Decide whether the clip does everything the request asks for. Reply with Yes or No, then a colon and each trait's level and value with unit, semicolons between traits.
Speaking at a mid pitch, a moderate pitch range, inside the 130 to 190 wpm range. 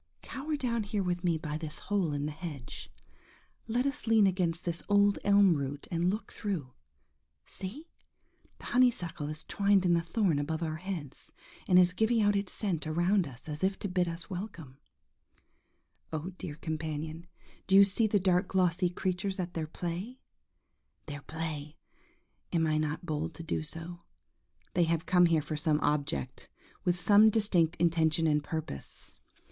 Yes: medium, 175 Hz; average, 4.0 semitones; average, 165 wpm